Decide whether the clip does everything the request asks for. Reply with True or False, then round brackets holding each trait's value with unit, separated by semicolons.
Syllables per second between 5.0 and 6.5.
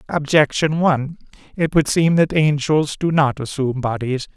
False (4.8 syllables/s)